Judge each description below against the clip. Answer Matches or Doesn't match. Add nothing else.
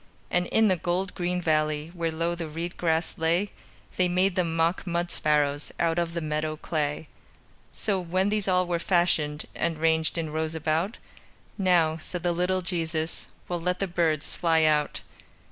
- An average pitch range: Doesn't match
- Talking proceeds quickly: Doesn't match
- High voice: Doesn't match